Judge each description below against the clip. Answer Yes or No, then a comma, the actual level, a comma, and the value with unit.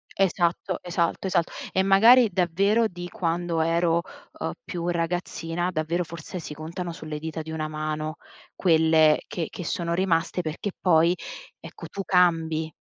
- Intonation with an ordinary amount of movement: No, narrow, 2.0 semitones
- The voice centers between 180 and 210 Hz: No, medium, 170 Hz